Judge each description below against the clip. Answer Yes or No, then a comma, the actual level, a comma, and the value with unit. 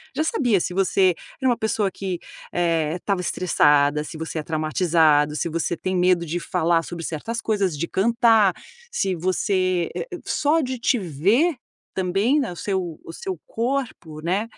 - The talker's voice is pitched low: No, medium, 185 Hz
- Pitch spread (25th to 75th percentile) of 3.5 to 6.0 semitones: Yes, average, 4.8 semitones